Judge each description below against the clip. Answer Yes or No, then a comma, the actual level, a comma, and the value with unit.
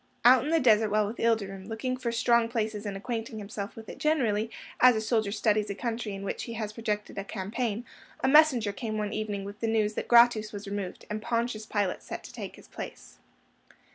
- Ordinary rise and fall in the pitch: No, narrow, 2.2 semitones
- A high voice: Yes, high, 220 Hz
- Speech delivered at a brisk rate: Yes, fast, 215 wpm